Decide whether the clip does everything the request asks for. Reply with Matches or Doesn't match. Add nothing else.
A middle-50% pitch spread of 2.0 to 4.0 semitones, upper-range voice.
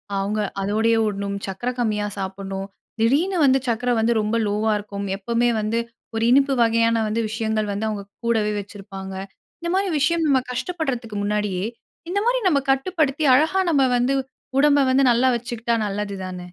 Doesn't match